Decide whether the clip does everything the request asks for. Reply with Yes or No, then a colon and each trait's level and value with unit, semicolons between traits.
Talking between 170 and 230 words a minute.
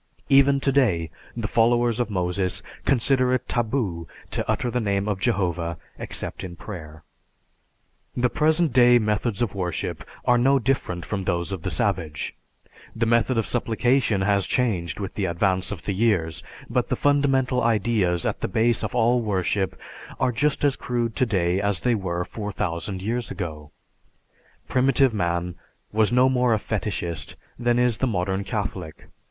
No: average, 160 wpm